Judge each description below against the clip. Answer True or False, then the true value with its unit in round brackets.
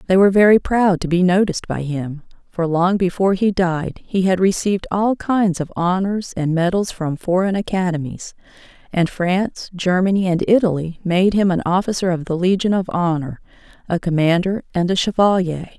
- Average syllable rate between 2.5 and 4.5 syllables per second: False (5.2 syllables/s)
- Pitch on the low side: False (180 Hz)